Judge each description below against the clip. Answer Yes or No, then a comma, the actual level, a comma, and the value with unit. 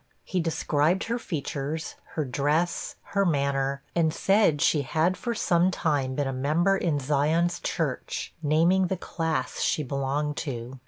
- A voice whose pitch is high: No, medium, 155 Hz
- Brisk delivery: No, average, 150 wpm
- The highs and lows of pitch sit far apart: No, average, 3.7 semitones